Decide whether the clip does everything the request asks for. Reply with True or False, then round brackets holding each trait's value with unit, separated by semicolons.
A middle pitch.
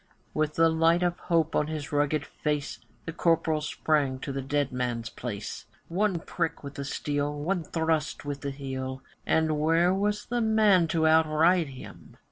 True (155 Hz)